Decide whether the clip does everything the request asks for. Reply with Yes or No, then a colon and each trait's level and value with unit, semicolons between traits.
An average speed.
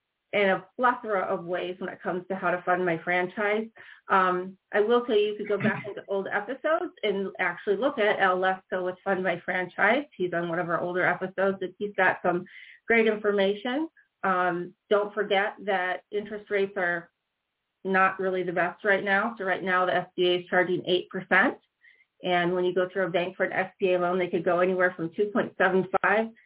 Yes: average, 195 wpm